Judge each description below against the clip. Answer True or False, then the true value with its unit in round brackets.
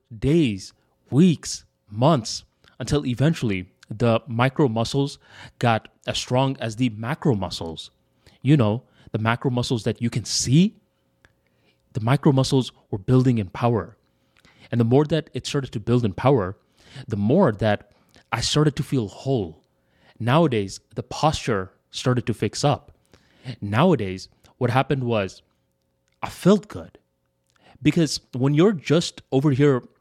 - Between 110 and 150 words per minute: True (140 wpm)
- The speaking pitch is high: False (125 Hz)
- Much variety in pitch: False (4.8 semitones)